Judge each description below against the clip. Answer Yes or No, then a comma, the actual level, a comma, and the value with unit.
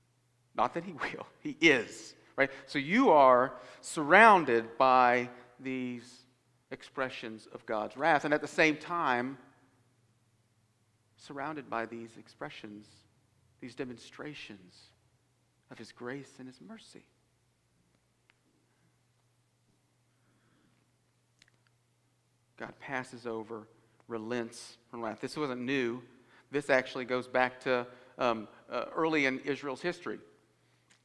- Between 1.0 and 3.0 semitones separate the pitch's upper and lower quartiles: Yes, narrow, 2.5 semitones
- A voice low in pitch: Yes, low, 125 Hz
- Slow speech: Yes, slow, 105 wpm